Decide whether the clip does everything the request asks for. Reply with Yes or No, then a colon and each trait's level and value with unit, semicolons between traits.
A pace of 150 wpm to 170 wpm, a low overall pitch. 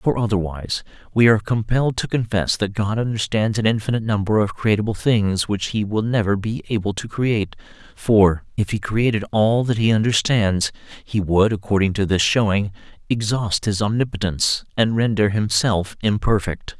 Yes: average, 160 wpm; low, 105 Hz